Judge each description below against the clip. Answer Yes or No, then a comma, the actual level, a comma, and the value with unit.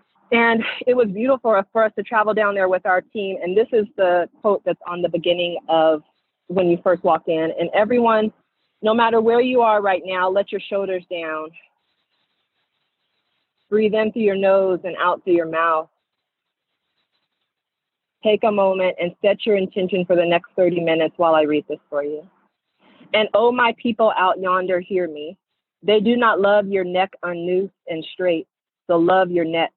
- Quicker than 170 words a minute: Yes, average, 185 wpm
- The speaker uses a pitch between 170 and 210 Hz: Yes, high, 190 Hz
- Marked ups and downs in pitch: No, average, 3.7 semitones